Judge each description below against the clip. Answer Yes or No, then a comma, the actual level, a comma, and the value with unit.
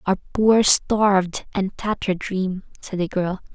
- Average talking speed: Yes, average, 150 wpm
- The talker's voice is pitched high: Yes, high, 195 Hz